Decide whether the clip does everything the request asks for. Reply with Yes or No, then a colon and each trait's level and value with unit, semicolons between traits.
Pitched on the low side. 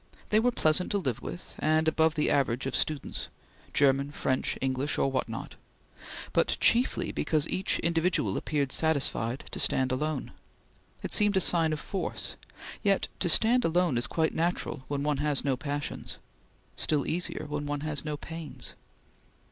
No: medium, 150 Hz